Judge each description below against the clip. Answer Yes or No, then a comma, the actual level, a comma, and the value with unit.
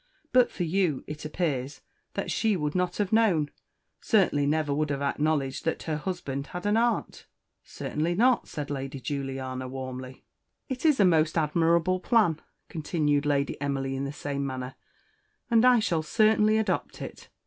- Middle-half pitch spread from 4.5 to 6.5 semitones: Yes, average, 5.1 semitones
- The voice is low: No, medium, 155 Hz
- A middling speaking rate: Yes, average, 160 wpm